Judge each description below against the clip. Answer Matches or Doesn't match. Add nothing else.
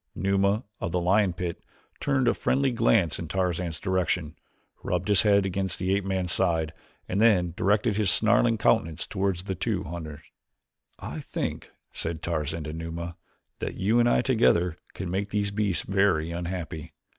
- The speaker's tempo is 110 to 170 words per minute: Matches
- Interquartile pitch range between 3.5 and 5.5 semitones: Doesn't match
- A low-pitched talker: Matches